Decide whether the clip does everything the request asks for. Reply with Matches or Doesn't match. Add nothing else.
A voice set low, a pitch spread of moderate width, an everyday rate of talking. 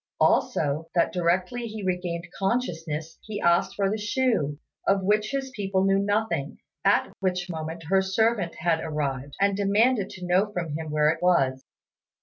Doesn't match